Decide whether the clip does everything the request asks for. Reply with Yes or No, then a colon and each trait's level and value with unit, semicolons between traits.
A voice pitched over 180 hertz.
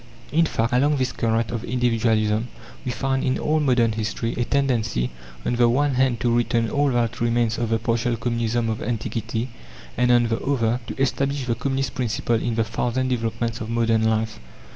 No: low, 120 Hz